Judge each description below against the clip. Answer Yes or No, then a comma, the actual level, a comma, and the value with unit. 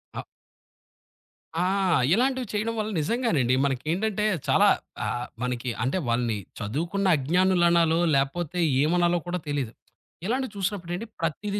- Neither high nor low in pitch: Yes, medium, 175 Hz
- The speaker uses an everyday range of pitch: No, wide, 6.8 semitones